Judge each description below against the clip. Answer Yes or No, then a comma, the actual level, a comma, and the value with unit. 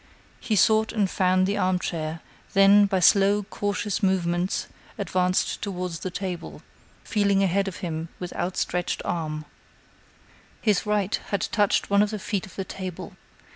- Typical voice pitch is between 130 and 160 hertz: No, high, 190 Hz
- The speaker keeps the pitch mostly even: Yes, narrow, 2.2 semitones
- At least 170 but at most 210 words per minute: No, average, 145 wpm